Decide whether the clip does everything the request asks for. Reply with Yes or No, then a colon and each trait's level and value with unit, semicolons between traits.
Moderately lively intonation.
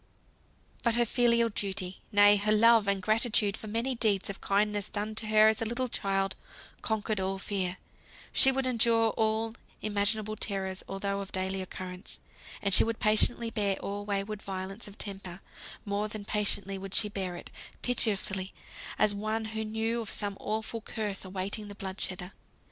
No: narrow, 2.1 semitones